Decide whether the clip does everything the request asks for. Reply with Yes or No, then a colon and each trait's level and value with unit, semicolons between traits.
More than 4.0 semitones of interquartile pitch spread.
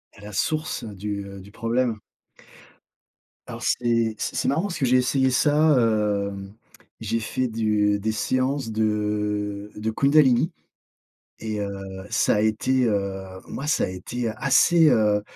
No: average, 3.7 semitones